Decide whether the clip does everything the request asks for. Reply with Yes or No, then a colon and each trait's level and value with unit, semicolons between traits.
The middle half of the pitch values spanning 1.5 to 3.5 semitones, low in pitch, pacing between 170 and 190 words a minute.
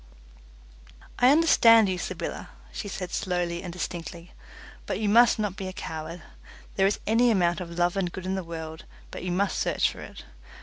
No: average, 3.0 semitones; medium, 185 Hz; average, 185 wpm